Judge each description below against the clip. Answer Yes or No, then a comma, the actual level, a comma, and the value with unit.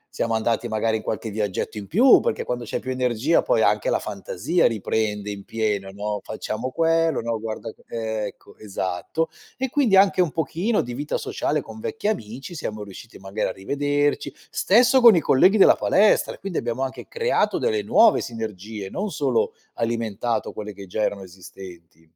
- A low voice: Yes, low, 115 Hz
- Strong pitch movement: Yes, wide, 8.0 semitones